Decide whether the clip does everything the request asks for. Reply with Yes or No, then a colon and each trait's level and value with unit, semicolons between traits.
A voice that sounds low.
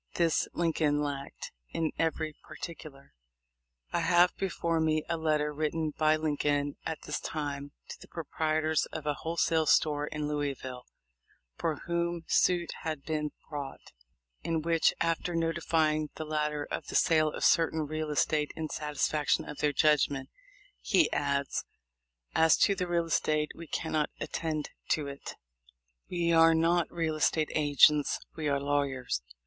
No: medium, 155 Hz